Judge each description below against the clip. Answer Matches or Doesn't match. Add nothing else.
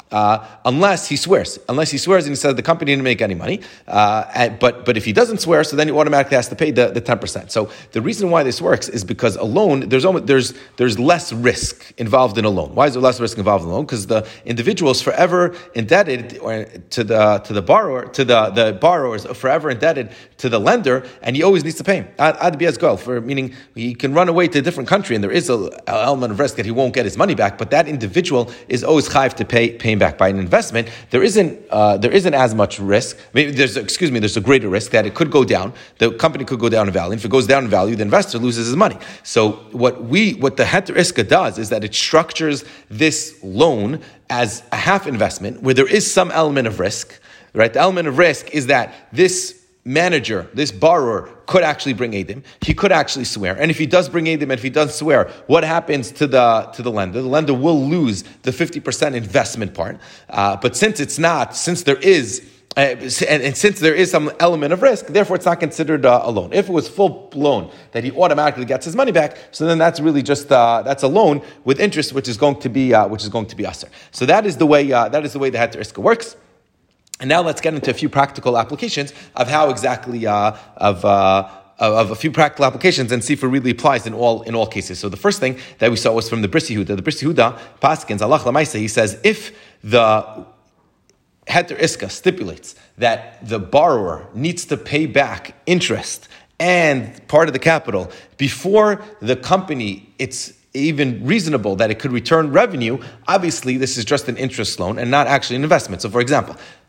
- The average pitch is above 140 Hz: Doesn't match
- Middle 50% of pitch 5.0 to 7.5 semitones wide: Matches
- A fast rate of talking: Matches